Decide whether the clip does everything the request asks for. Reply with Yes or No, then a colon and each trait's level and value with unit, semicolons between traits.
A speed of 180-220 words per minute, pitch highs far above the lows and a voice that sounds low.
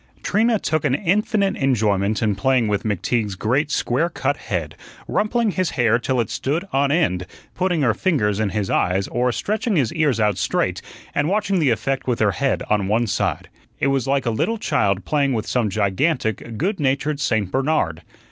Yes: average, 185 wpm; wide, 6.6 semitones; low, 130 Hz